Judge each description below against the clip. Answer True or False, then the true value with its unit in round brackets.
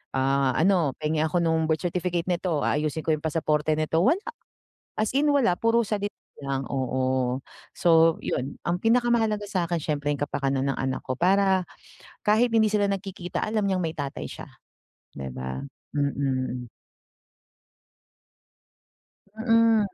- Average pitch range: False (6.6 semitones)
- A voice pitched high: False (165 Hz)